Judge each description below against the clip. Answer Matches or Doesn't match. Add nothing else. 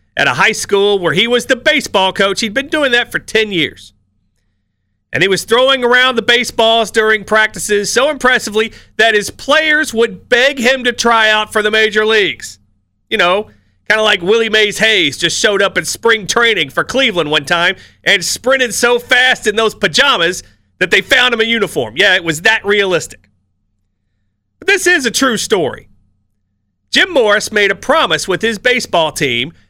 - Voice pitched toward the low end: Doesn't match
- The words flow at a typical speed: Matches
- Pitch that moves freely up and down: Matches